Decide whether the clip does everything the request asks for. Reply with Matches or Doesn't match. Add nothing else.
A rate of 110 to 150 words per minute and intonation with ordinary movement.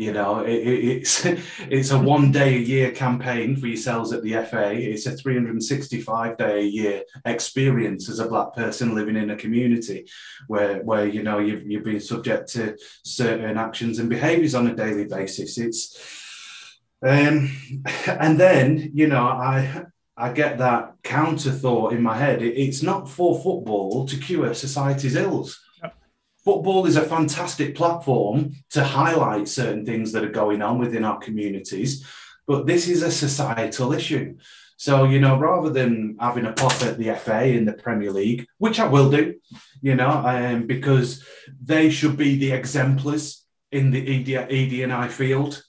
Doesn't match